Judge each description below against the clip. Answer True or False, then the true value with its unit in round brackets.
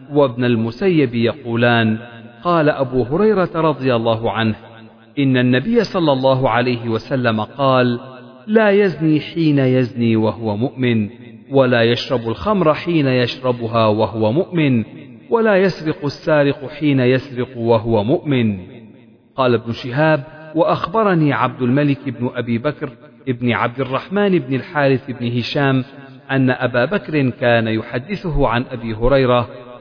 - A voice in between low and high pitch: False (130 Hz)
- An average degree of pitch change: True (3.9 semitones)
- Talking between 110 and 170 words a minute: True (120 wpm)